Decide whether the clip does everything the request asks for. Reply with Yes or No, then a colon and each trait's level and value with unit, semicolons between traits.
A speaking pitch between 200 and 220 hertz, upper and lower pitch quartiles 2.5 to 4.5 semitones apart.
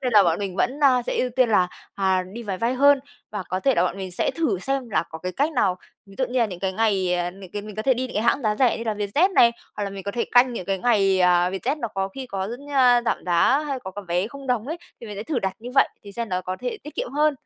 No: high, 215 Hz; average, 5.0 semitones